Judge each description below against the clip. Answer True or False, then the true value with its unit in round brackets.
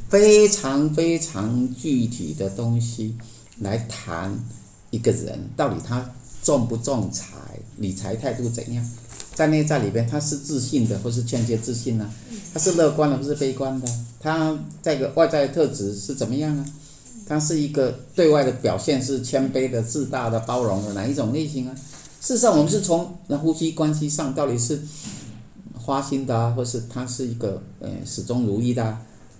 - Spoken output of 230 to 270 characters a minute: True (255 characters per minute)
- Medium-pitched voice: False (130 Hz)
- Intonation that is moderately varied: True (4.3 semitones)